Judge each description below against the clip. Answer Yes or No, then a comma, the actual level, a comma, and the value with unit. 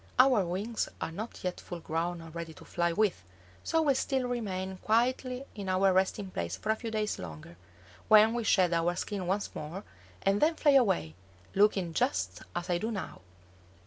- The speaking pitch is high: Yes, high, 195 Hz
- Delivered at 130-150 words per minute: No, average, 185 wpm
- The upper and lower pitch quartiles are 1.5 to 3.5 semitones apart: No, average, 4.4 semitones